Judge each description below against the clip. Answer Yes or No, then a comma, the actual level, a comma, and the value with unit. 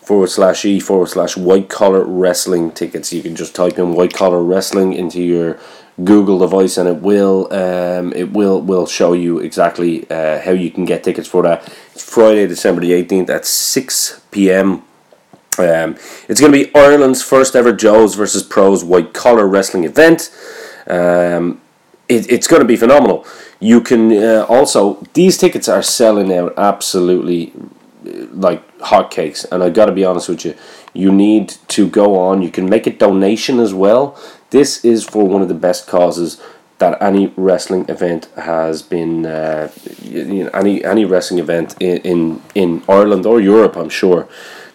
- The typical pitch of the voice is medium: No, very low, 95 Hz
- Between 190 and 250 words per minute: No, average, 175 wpm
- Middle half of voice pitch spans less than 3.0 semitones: Yes, narrow, 2.6 semitones